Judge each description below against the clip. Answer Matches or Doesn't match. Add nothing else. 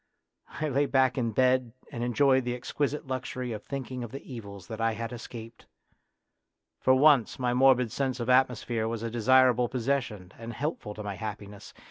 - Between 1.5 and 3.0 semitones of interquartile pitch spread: Matches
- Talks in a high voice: Doesn't match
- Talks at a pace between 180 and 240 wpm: Matches